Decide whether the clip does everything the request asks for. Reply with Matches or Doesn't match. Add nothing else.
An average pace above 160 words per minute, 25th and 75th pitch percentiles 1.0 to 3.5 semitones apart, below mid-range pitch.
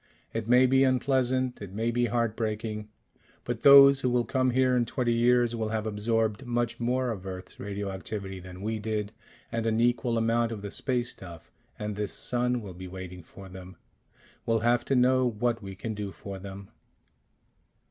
Matches